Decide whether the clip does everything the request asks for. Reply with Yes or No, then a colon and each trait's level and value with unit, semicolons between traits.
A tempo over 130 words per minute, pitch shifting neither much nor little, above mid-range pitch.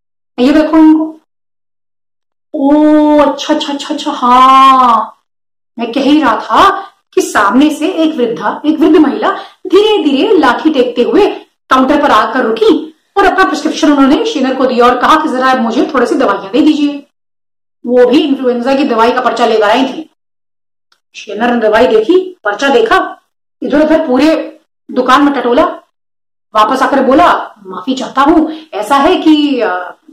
Yes: average, 155 wpm; average, 4.3 semitones; very high, 285 Hz